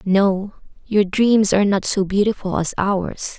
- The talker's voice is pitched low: No, high, 195 Hz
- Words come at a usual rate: Yes, average, 160 wpm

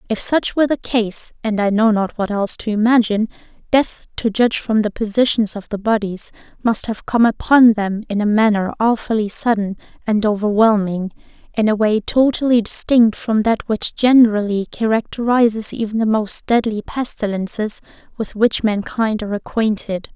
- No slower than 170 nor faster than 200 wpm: No, average, 160 wpm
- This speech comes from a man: No, female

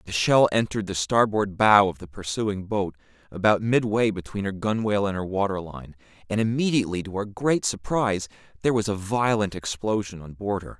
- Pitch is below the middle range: Yes, low, 100 Hz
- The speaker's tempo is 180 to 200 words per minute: Yes, average, 185 wpm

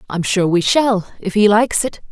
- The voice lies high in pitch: Yes, high, 205 Hz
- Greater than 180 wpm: Yes, average, 200 wpm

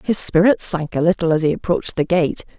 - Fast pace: Yes, fast, 230 wpm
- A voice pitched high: No, medium, 170 Hz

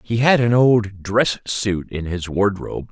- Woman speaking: No, male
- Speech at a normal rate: Yes, average, 185 wpm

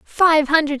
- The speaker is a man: No, female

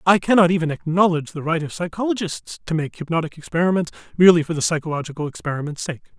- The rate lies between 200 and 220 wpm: No, average, 175 wpm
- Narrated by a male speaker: Yes, male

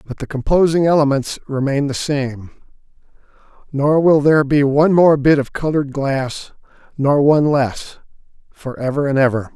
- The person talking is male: Yes, male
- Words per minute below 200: Yes, average, 150 wpm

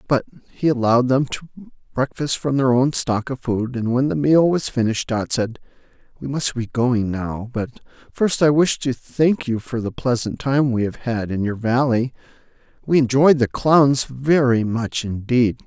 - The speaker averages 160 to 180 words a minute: No, average, 190 wpm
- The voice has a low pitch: Yes, low, 130 Hz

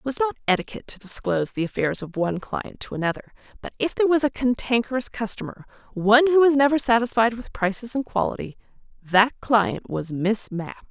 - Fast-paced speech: No, average, 185 wpm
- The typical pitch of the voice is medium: No, high, 230 Hz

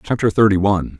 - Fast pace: No, average, 180 wpm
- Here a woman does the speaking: No, male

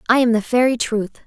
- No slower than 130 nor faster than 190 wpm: No, fast, 235 wpm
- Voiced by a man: No, female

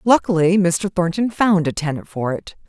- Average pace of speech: Yes, average, 180 wpm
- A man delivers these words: No, female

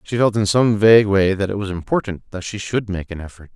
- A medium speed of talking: No, fast, 270 wpm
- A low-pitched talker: Yes, low, 100 Hz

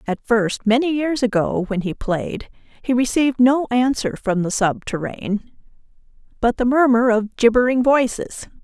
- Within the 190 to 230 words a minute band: No, average, 145 wpm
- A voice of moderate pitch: No, high, 235 Hz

